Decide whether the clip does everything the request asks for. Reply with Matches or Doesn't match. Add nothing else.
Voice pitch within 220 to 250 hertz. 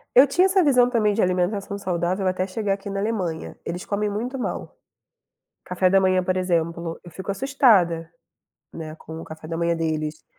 Doesn't match